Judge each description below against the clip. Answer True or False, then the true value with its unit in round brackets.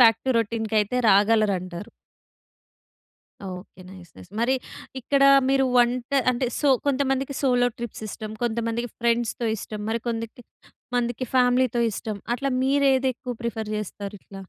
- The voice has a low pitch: False (235 Hz)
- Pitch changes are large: False (2.9 semitones)